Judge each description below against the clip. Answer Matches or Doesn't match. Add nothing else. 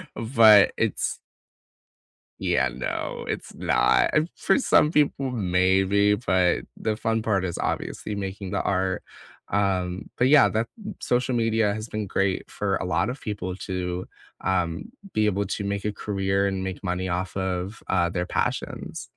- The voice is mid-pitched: Doesn't match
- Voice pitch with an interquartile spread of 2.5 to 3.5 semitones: Matches